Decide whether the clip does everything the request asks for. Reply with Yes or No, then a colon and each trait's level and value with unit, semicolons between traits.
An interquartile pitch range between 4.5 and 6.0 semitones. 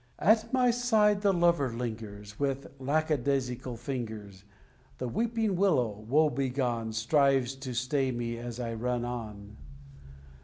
Yes: average, 5.1 semitones